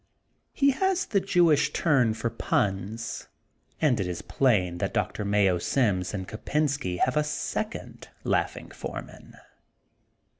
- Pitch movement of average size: No, wide, 7.6 semitones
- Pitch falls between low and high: No, low, 115 Hz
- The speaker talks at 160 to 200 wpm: No, slow, 135 wpm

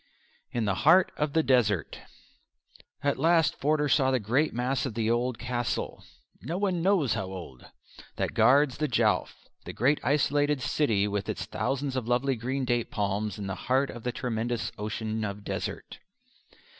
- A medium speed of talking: Yes, average, 170 wpm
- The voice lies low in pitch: Yes, low, 125 Hz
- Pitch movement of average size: Yes, average, 4.6 semitones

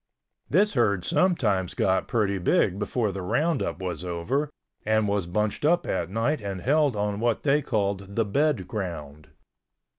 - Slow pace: No, average, 155 wpm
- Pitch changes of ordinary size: No, wide, 6.0 semitones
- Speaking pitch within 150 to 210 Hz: No, low, 105 Hz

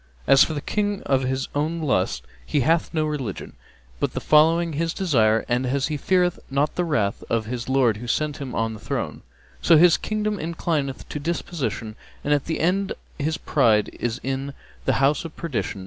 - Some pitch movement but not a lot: Yes, average, 4.6 semitones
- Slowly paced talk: No, average, 195 wpm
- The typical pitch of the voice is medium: Yes, medium, 145 Hz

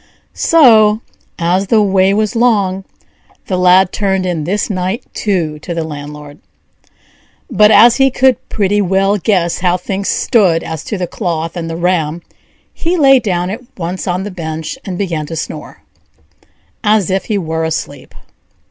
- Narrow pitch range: No, average, 3.7 semitones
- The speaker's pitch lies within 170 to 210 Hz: Yes, medium, 185 Hz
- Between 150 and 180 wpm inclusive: Yes, average, 165 wpm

